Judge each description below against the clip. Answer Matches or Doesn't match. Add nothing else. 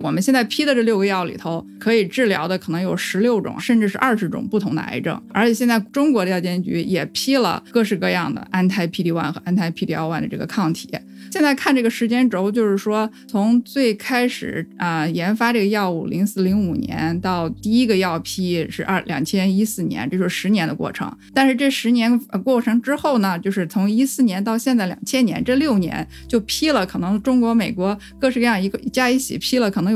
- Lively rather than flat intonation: Doesn't match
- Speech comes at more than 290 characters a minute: Matches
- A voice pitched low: Doesn't match